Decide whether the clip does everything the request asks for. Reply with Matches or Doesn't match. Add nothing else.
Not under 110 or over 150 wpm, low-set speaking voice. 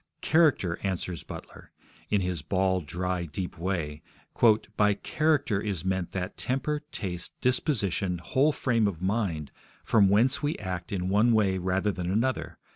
Matches